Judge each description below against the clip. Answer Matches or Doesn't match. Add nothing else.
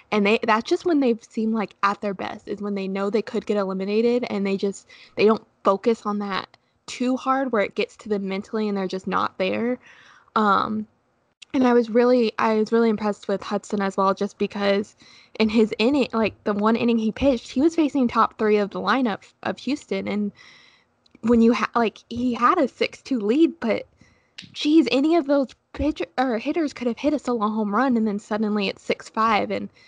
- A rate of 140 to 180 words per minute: Doesn't match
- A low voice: Doesn't match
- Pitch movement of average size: Matches